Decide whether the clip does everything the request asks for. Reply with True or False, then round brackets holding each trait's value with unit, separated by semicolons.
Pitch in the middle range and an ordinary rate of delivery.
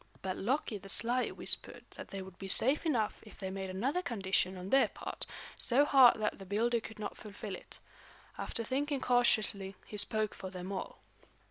False (215 Hz; 190 wpm)